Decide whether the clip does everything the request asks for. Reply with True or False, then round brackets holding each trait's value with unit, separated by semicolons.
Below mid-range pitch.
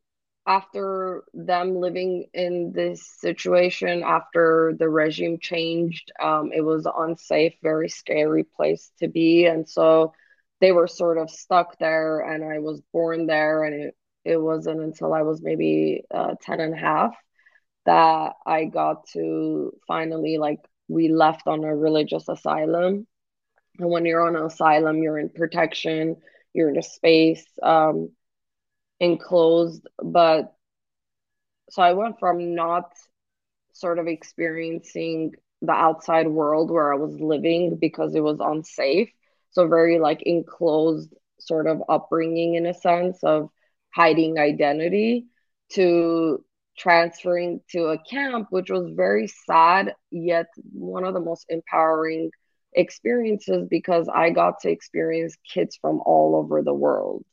False (165 Hz)